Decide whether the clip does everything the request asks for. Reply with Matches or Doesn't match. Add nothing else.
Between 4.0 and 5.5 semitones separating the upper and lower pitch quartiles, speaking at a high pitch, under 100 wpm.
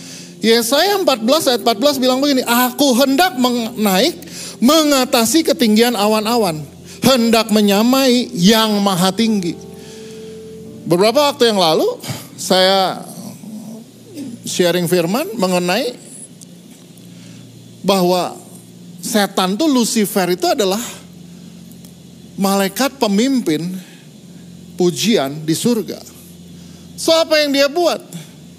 Matches